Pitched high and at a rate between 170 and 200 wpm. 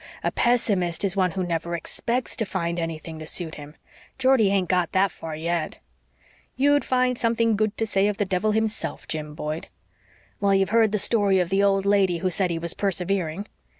Yes: high, 195 Hz; average, 195 wpm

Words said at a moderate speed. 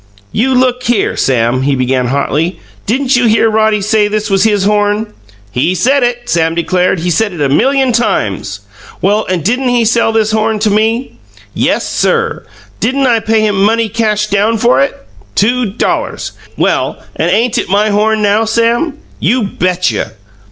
Yes: average, 175 wpm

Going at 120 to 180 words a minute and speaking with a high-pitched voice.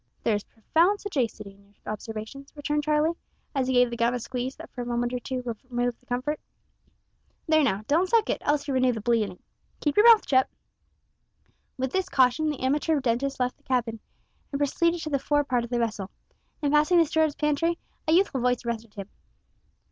No: average, 200 wpm; very high, 260 Hz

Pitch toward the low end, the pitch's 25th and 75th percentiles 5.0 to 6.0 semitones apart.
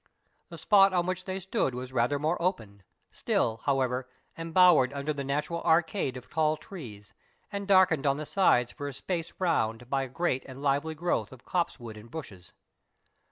No: medium, 145 Hz; wide, 5.5 semitones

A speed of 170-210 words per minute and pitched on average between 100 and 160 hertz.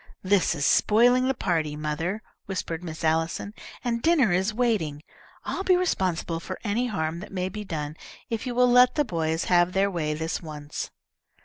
No: average, 180 wpm; medium, 185 Hz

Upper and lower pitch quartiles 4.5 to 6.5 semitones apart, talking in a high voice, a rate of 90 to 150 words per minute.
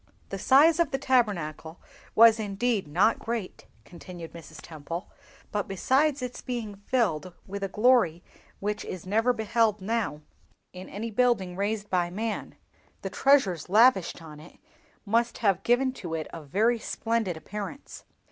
Yes: average, 4.8 semitones; high, 210 Hz; average, 145 wpm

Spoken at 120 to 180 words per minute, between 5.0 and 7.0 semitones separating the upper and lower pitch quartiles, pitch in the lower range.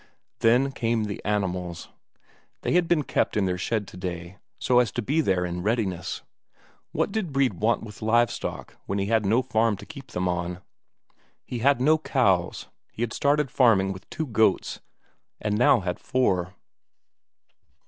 Yes: average, 170 wpm; average, 5.3 semitones; low, 110 Hz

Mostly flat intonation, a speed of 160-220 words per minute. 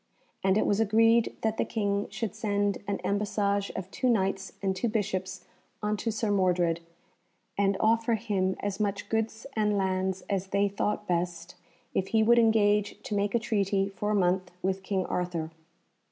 Yes: narrow, 2.2 semitones; average, 170 wpm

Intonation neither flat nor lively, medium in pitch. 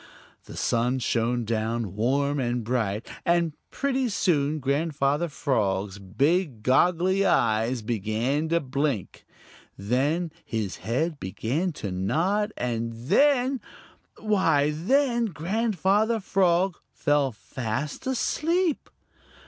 No: wide, 8.1 semitones; medium, 145 Hz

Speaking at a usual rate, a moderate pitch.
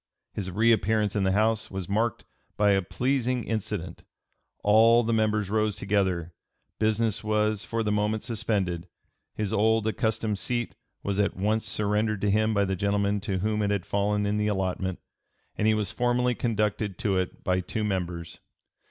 No: average, 170 wpm; low, 105 Hz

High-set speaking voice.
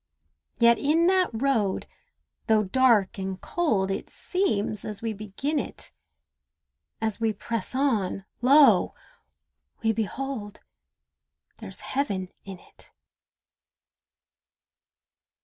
Yes: high, 225 Hz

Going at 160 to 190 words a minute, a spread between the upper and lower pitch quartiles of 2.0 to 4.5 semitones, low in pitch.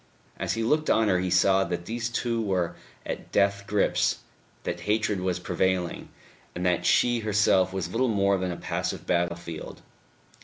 Yes: average, 165 wpm; average, 3.3 semitones; very low, 95 Hz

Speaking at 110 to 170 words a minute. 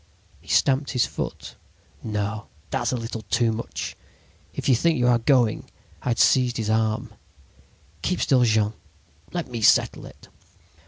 Yes: average, 155 wpm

